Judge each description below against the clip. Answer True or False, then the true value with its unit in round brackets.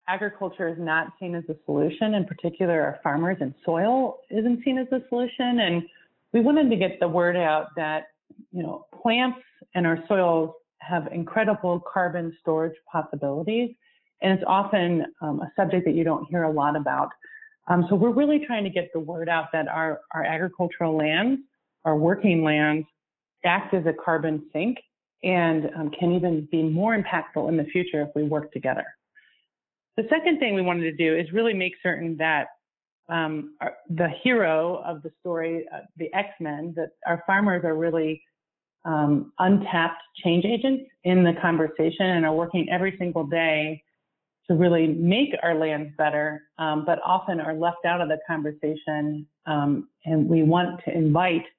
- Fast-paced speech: False (175 wpm)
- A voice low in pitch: False (170 Hz)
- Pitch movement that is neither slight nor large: True (3.2 semitones)